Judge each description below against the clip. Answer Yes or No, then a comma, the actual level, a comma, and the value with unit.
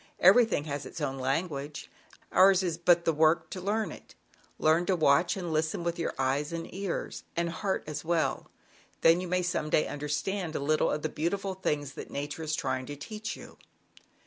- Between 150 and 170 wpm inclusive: No, average, 200 wpm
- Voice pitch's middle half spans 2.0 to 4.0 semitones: Yes, average, 3.6 semitones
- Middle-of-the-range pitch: Yes, medium, 165 Hz